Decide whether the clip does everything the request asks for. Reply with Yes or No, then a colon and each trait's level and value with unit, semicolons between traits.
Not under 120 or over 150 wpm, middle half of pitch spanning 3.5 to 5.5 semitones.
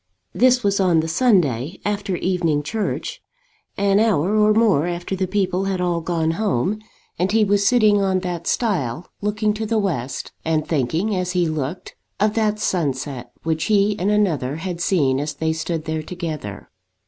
No: average, 170 wpm; average, 4.5 semitones